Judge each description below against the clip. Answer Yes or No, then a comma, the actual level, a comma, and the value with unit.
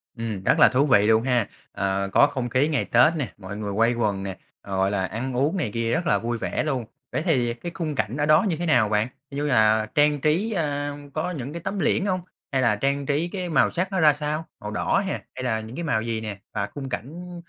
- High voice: No, low, 130 Hz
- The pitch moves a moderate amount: No, wide, 5.9 semitones